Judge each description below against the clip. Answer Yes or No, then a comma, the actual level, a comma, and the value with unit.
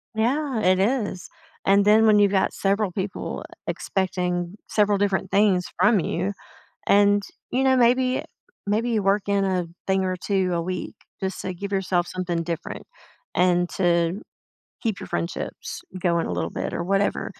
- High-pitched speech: Yes, high, 195 Hz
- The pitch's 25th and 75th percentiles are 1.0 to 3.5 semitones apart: Yes, narrow, 2.5 semitones